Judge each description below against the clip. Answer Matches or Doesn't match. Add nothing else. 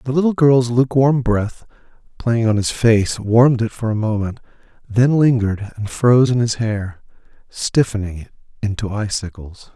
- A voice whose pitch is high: Doesn't match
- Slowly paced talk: Doesn't match